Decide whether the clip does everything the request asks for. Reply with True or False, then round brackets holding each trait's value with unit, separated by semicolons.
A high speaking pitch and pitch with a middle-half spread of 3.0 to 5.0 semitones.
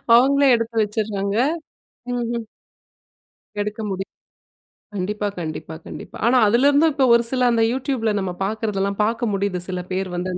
True (215 Hz; 3.4 semitones)